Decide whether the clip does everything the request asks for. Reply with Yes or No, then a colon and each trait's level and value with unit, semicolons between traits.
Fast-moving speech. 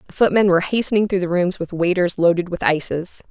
Yes: fast, 220 wpm